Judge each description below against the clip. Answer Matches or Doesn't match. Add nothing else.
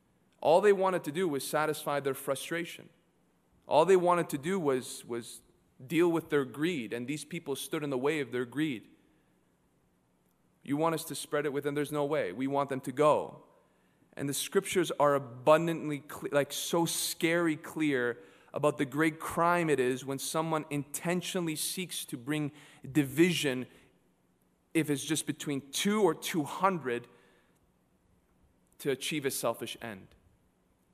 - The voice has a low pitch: Doesn't match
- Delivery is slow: Doesn't match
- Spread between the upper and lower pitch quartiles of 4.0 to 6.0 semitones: Doesn't match